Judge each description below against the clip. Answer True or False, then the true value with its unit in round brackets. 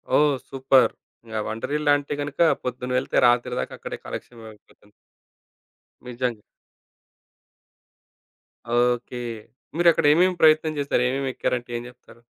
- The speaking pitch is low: True (125 Hz)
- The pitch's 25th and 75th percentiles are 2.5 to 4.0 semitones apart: True (3.2 semitones)